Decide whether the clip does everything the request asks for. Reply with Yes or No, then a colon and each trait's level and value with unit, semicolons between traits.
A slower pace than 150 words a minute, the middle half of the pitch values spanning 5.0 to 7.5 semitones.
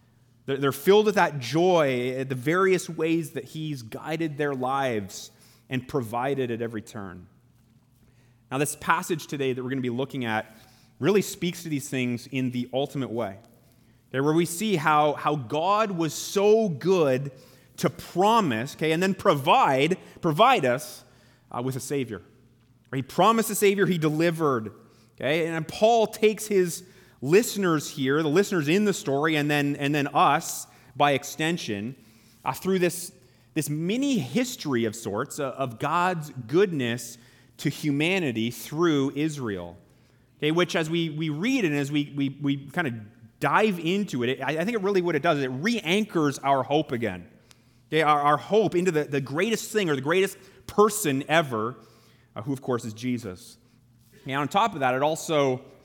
No: average, 170 wpm; wide, 5.6 semitones